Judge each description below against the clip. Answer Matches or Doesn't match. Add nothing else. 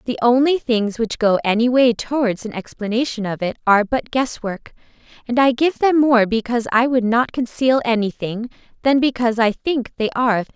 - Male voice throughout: Doesn't match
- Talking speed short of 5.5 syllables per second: Doesn't match